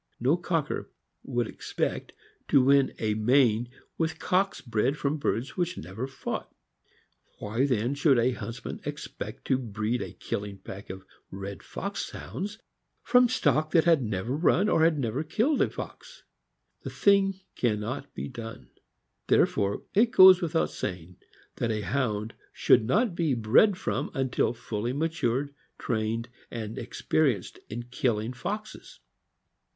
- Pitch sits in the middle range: No, low, 130 Hz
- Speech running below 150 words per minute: Yes, average, 140 wpm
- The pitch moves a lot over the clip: Yes, wide, 6.5 semitones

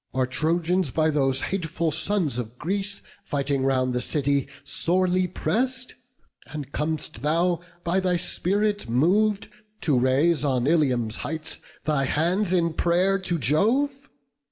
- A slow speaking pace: Yes, slow, 130 wpm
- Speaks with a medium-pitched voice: Yes, medium, 160 Hz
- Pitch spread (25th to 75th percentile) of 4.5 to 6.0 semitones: Yes, average, 5.1 semitones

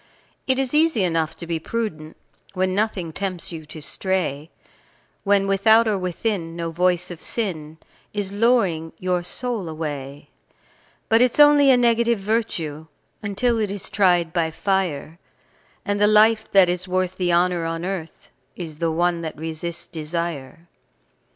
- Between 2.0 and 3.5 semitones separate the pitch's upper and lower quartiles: No, average, 4.3 semitones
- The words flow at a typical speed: Yes, average, 150 wpm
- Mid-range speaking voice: Yes, medium, 180 Hz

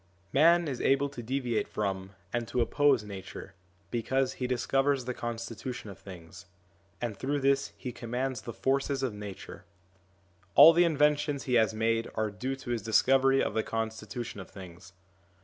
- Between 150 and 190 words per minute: Yes, average, 165 wpm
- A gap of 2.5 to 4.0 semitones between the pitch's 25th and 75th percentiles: Yes, average, 3.6 semitones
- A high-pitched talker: No, low, 120 Hz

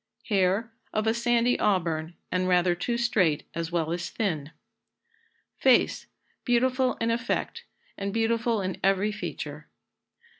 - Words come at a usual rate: No, slow, 125 wpm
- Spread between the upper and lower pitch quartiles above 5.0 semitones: No, average, 4.7 semitones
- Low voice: No, high, 205 Hz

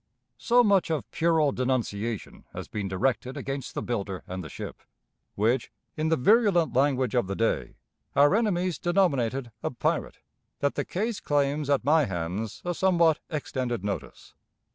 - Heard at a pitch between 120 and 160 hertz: Yes, low, 135 Hz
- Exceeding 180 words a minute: No, average, 155 wpm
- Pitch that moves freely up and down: Yes, wide, 6.4 semitones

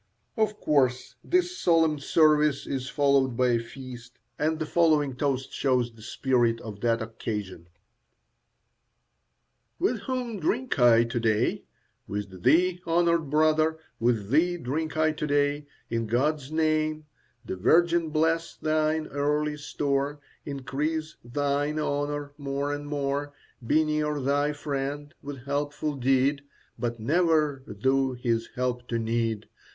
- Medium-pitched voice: Yes, medium, 145 Hz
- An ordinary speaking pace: No, slow, 130 wpm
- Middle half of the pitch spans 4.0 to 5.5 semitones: No, average, 3.6 semitones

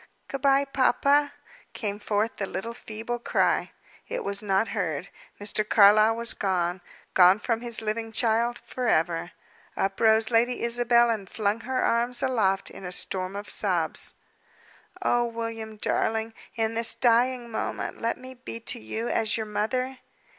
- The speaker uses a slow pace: No, average, 155 wpm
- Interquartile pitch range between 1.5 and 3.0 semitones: Yes, average, 2.7 semitones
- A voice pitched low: No, high, 225 Hz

